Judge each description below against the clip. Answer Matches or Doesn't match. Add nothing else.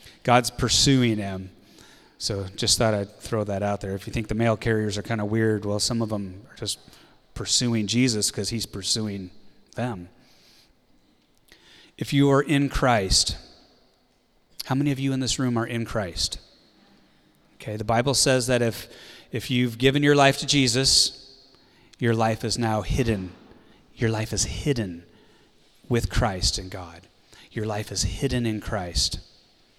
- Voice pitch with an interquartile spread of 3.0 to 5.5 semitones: Matches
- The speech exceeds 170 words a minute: Doesn't match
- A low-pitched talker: Matches